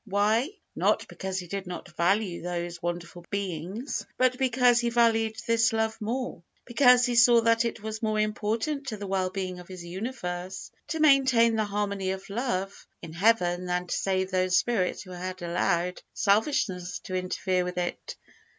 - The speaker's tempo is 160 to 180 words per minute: Yes, average, 170 wpm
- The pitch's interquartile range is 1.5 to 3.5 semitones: No, average, 4.2 semitones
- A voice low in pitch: No, high, 200 Hz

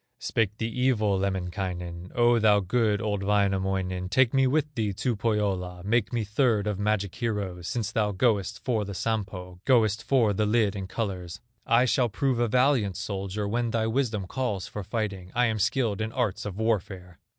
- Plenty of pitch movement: No, average, 3.3 semitones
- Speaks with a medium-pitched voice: No, low, 105 Hz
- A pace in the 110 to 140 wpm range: No, average, 180 wpm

